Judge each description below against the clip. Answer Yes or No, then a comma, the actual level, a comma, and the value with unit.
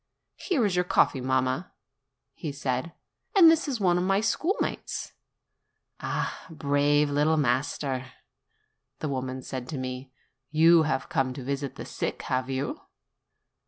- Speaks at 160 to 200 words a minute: No, average, 140 wpm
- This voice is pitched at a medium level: Yes, medium, 145 Hz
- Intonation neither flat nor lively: Yes, average, 4.9 semitones